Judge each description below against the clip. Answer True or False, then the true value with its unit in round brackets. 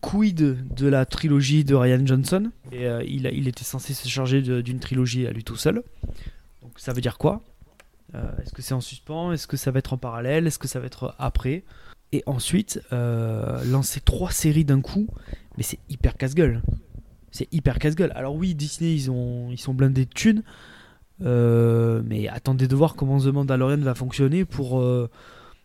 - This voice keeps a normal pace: True (195 wpm)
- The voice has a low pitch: True (130 Hz)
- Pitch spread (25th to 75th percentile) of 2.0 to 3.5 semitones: True (2.6 semitones)